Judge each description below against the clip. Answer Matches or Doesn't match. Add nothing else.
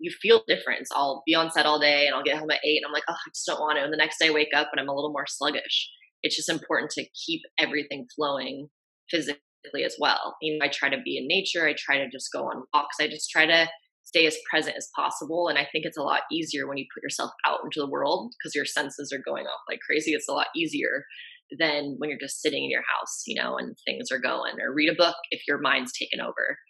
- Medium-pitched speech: Matches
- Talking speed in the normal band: Doesn't match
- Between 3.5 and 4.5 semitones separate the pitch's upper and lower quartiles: Doesn't match